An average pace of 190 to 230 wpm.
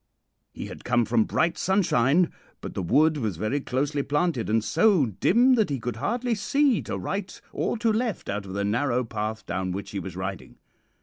Yes: average, 195 wpm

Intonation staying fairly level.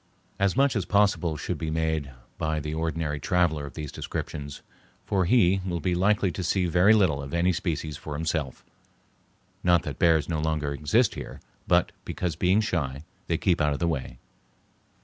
No: average, 3.3 semitones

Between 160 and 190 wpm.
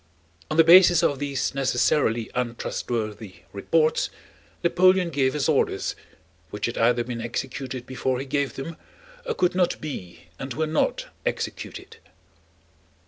No: slow, 135 wpm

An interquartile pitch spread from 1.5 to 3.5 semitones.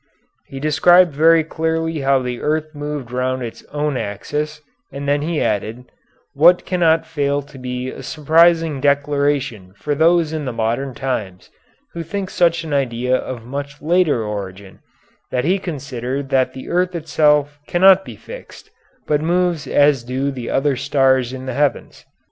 No: average, 3.9 semitones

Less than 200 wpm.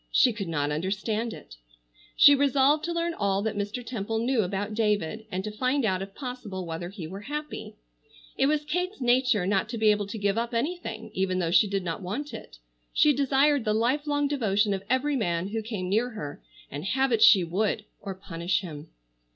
No: fast, 205 wpm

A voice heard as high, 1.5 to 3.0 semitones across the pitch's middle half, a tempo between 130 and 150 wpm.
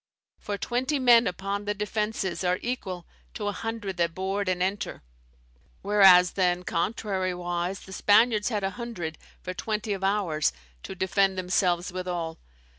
Yes: high, 195 Hz; narrow, 2.6 semitones; average, 145 wpm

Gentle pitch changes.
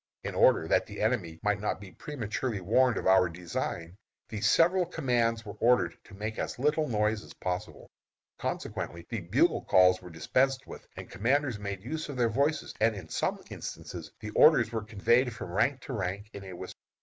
No: average, 5.1 semitones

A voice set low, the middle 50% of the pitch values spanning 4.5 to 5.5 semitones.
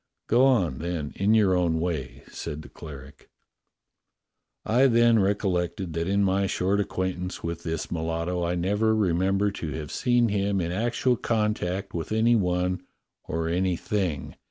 No: very low, 95 Hz; average, 3.7 semitones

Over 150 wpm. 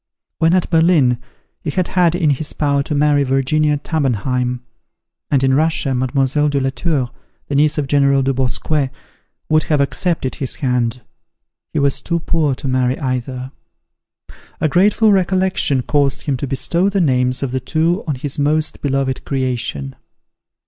Yes: average, 160 wpm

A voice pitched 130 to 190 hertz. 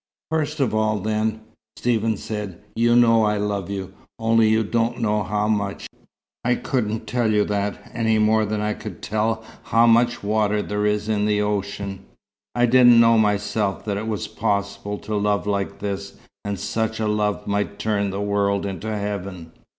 No: low, 105 Hz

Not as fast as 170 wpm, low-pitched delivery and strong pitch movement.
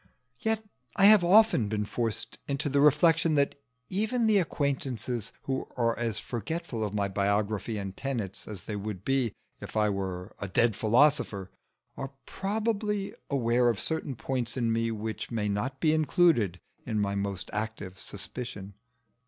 Yes: average, 155 wpm; low, 120 Hz; wide, 6.3 semitones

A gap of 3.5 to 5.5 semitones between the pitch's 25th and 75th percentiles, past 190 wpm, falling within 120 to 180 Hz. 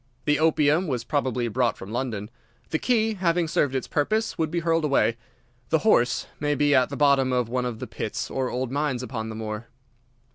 Yes: average, 4.3 semitones; fast, 205 wpm; low, 135 Hz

